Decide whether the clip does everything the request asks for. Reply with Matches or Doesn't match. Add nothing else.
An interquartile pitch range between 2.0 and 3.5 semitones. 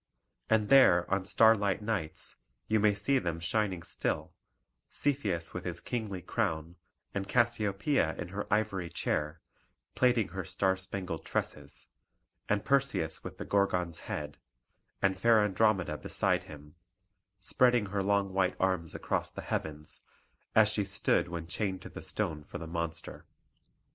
Doesn't match